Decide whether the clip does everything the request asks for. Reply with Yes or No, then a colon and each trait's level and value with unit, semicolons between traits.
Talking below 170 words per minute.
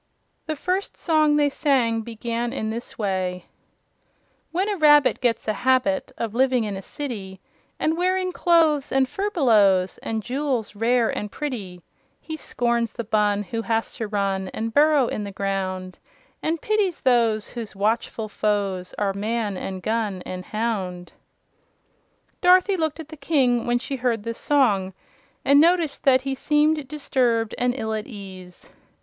Yes: average, 155 wpm